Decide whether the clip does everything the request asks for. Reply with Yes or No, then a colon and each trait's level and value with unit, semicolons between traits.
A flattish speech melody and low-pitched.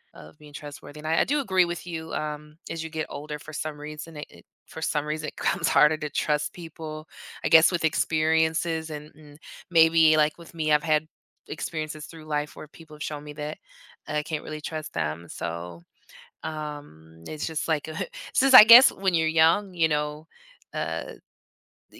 No: narrow, 1.4 semitones; medium, 155 Hz